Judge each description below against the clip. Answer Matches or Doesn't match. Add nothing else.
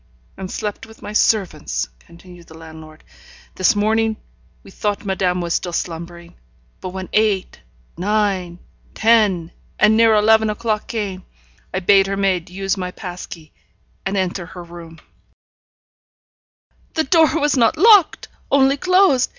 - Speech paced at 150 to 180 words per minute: Doesn't match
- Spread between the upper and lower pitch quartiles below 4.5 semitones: Matches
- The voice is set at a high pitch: Matches